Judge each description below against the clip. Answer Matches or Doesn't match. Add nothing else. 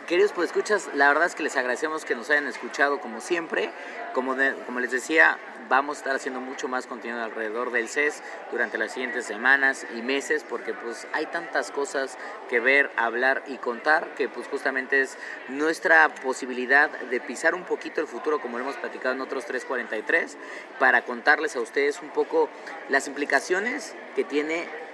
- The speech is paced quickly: Doesn't match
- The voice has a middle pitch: Matches